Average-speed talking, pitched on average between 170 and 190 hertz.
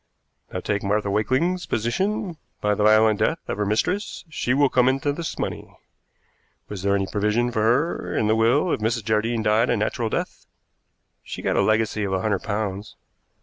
No: average, 190 wpm; low, 110 Hz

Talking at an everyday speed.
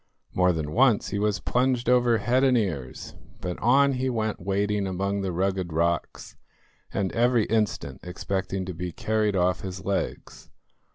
Yes: average, 160 wpm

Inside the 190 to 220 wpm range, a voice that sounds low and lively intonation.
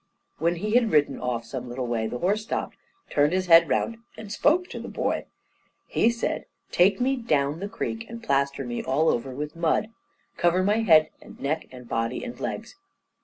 No: average, 200 wpm; medium, 165 Hz; wide, 7.9 semitones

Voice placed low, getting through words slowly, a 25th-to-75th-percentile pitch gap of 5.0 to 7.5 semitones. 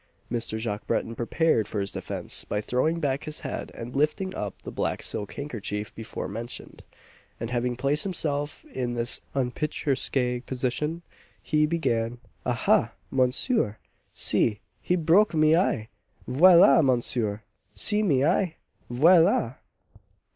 Yes: low, 130 Hz; slow, 130 wpm; average, 5.3 semitones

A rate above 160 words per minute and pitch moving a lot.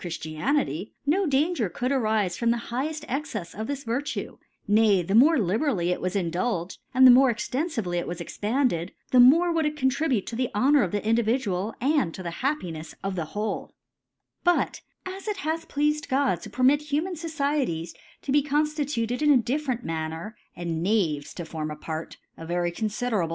Yes: average, 190 wpm; wide, 8.2 semitones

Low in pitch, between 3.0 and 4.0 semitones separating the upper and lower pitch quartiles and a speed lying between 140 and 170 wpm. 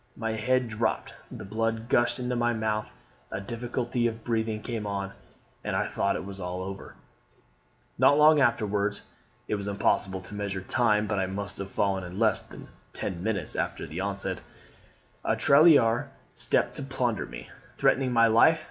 Yes: low, 110 Hz; average, 3.3 semitones; average, 165 wpm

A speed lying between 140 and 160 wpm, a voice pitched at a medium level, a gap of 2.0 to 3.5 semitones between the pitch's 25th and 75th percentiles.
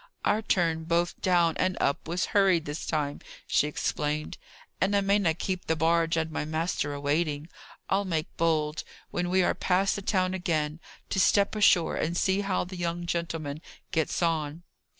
No: average, 175 wpm; medium, 170 Hz; average, 2.9 semitones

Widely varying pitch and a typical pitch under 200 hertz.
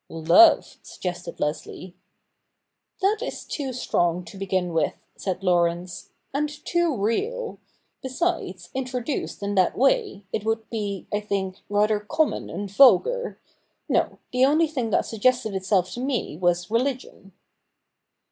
No: wide, 6.4 semitones; high, 210 Hz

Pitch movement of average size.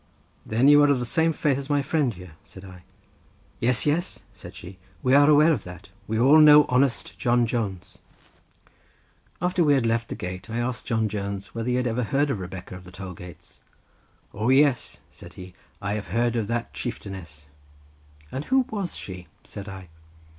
No: wide, 6.5 semitones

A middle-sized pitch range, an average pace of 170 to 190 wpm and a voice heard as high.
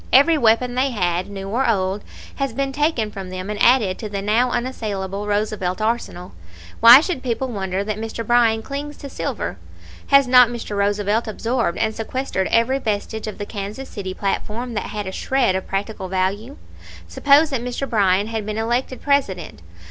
Yes: average, 3.9 semitones; average, 180 wpm; high, 220 Hz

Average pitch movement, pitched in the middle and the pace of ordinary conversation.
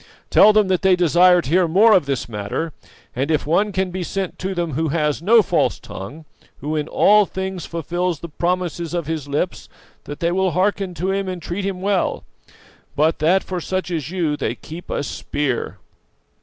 Yes: average, 3.3 semitones; medium, 175 Hz; average, 195 wpm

